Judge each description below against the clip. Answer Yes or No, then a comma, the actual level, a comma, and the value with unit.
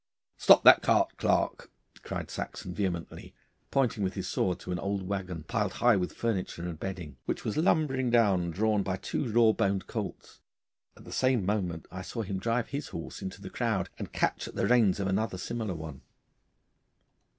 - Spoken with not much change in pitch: No, average, 3.9 semitones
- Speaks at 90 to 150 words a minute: No, average, 185 wpm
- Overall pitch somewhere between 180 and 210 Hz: No, low, 100 Hz